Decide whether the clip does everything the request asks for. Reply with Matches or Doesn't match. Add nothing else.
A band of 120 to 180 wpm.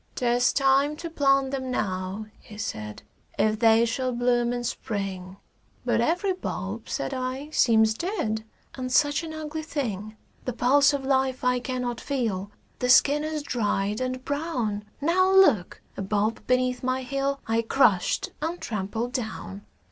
Matches